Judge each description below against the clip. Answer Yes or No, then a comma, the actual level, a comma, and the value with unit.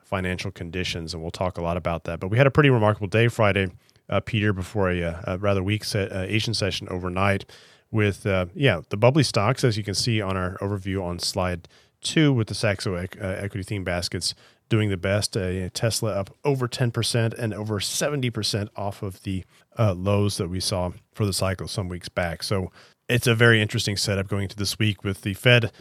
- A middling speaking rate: No, fast, 210 wpm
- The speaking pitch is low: Yes, low, 100 Hz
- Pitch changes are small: No, average, 3.2 semitones